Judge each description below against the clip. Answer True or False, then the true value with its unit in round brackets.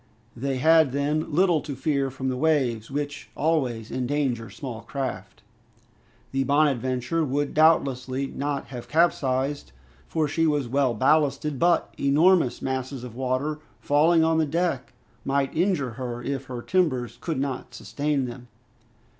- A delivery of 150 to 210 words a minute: False (140 wpm)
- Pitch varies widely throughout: False (3.2 semitones)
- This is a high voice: False (140 Hz)